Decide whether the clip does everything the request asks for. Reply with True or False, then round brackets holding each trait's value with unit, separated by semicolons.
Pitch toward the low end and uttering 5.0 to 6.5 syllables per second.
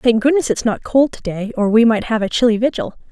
False (230 Hz; 5.8 syllables/s)